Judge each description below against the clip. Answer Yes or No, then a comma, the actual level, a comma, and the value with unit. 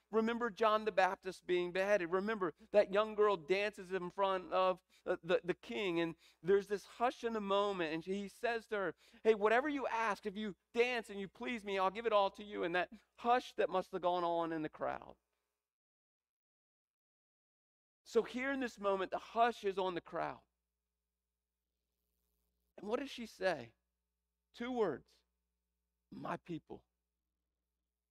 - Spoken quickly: No, average, 165 wpm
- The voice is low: No, medium, 185 Hz